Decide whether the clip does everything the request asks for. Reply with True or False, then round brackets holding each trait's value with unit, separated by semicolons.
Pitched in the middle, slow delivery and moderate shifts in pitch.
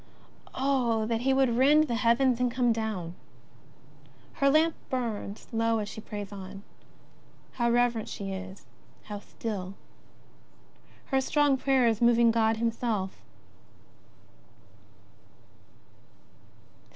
False (230 Hz; 110 wpm; 3.4 semitones)